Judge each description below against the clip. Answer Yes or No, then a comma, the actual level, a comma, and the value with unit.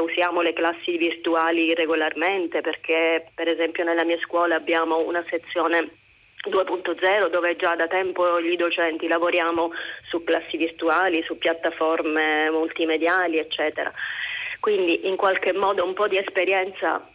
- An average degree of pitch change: No, narrow, 1.3 semitones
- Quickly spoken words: No, average, 130 wpm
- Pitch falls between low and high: Yes, medium, 170 Hz